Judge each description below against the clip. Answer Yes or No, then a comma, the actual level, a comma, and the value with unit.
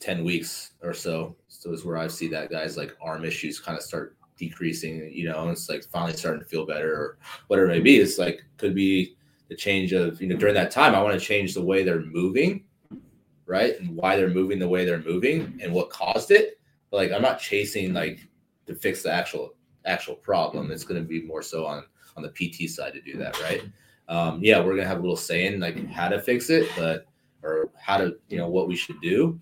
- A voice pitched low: Yes, very low, 95 Hz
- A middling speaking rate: No, fast, 235 wpm